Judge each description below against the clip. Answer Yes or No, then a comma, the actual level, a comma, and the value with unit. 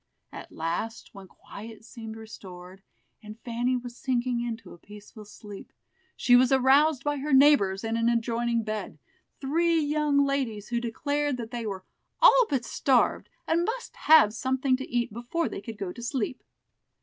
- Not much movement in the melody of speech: No, average, 4.0 semitones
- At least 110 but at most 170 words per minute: Yes, average, 165 wpm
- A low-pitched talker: No, high, 240 Hz